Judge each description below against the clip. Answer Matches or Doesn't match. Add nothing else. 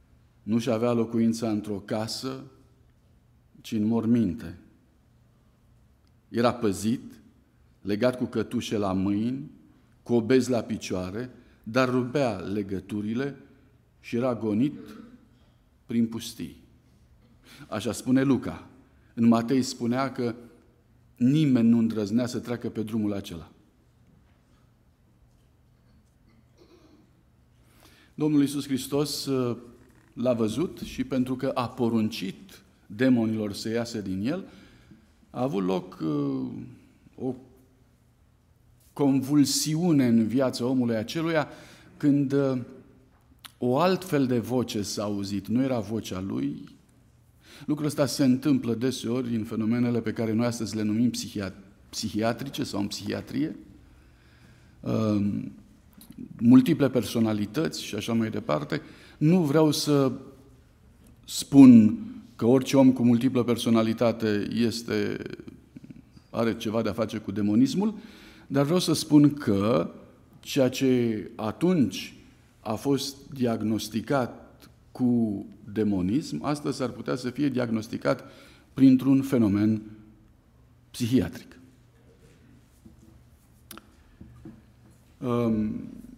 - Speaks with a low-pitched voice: Matches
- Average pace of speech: Doesn't match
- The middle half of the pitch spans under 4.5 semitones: Matches